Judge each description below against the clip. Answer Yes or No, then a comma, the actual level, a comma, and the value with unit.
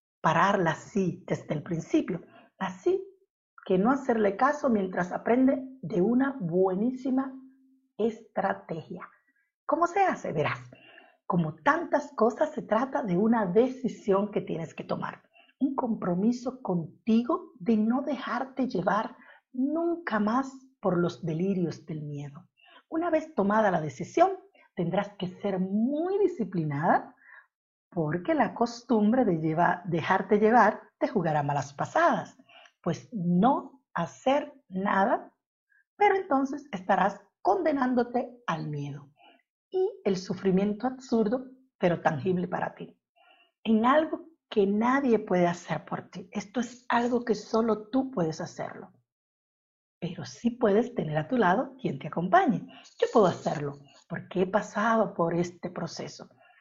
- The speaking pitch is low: No, high, 220 Hz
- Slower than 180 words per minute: Yes, slow, 125 wpm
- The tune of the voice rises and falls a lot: Yes, wide, 6.7 semitones